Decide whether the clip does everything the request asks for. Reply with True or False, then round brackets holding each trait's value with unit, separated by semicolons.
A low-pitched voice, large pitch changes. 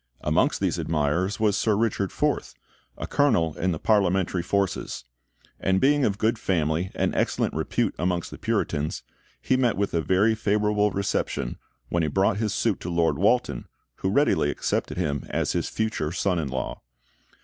False (95 Hz; 4.0 semitones)